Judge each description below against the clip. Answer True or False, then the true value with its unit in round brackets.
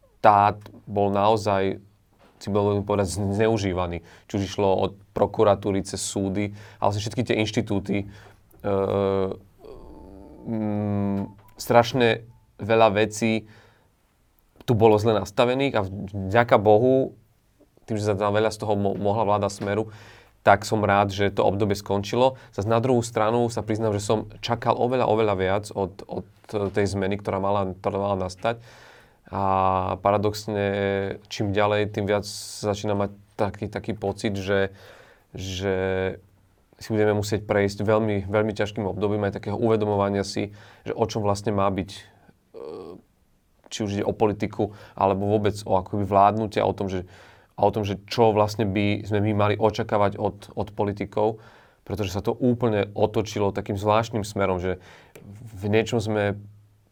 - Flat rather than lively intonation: True (1.7 semitones)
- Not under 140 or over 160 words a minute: True (145 wpm)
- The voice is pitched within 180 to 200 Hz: False (105 Hz)